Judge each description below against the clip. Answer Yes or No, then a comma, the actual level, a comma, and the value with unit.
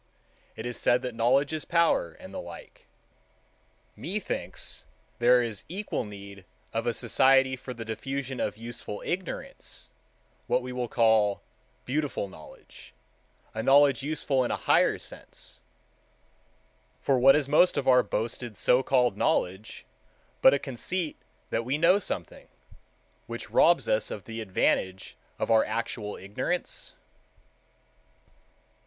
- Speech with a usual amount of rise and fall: Yes, average, 4.0 semitones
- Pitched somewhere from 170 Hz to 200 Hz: No, low, 125 Hz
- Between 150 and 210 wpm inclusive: No, slow, 135 wpm